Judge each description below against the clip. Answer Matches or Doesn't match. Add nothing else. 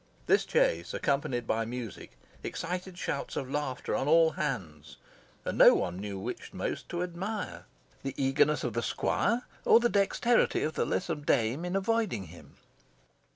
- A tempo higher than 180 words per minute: Doesn't match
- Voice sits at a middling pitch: Matches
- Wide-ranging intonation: Matches